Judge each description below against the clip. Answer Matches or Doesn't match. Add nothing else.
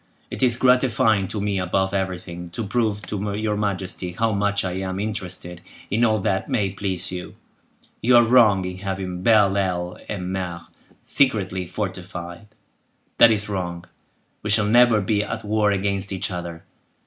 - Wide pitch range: Doesn't match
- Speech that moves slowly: Doesn't match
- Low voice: Matches